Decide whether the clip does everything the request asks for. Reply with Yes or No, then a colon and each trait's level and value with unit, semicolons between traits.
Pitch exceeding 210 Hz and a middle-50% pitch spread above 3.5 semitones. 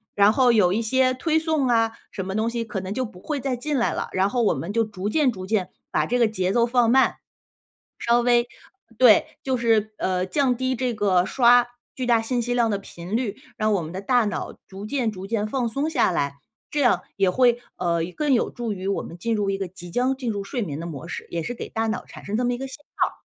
Yes: high, 225 Hz; average, 4.2 semitones